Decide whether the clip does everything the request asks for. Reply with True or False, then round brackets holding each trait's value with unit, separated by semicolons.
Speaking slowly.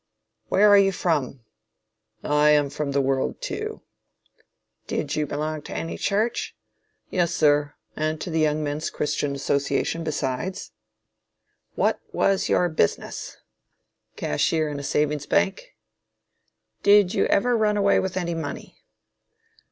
True (130 wpm)